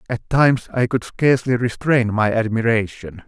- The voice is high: No, low, 115 Hz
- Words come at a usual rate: Yes, average, 145 wpm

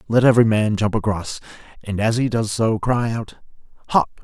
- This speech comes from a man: Yes, male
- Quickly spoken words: No, average, 185 wpm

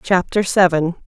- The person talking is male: No, female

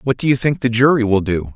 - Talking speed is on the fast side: Yes, fast, 310 wpm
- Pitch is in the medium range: No, low, 120 Hz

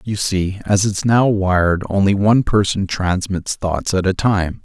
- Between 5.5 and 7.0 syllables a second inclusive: No, 4.5 syllables/s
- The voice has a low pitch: Yes, low, 100 Hz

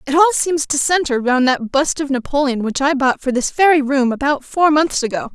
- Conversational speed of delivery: No, fast, 235 wpm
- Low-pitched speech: No, very high, 280 Hz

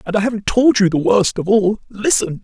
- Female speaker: No, male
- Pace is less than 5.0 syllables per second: No, 5.4 syllables/s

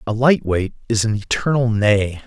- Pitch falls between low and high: No, low, 110 Hz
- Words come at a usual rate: Yes, average, 185 wpm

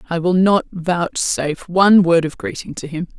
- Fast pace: No, average, 190 wpm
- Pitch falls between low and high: Yes, medium, 180 Hz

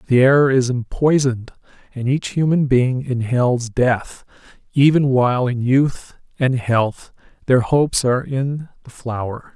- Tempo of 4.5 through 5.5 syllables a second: No, 4.2 syllables/s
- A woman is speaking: No, male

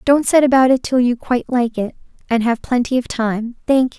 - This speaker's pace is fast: Yes, fast, 240 wpm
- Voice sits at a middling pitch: No, high, 245 Hz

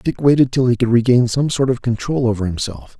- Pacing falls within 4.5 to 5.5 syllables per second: No, 5.8 syllables/s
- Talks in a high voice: No, low, 125 Hz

